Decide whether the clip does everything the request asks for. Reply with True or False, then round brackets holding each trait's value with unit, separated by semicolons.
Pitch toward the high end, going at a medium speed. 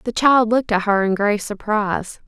False (210 Hz; 210 wpm)